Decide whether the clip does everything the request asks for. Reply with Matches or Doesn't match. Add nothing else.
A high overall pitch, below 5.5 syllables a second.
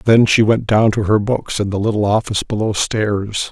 Doesn't match